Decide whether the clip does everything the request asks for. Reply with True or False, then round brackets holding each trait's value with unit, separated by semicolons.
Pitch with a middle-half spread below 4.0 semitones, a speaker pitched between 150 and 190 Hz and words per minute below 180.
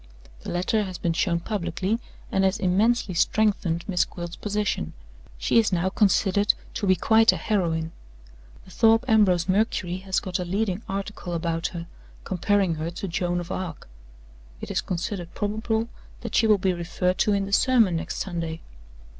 True (3.3 semitones; 185 Hz; 170 wpm)